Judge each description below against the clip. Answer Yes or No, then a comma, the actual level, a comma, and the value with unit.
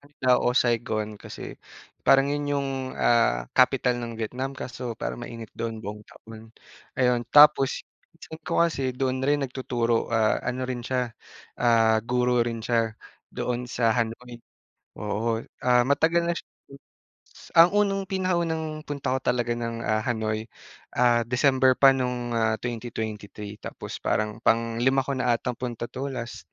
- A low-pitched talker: Yes, low, 125 Hz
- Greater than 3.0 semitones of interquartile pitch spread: No, narrow, 2.6 semitones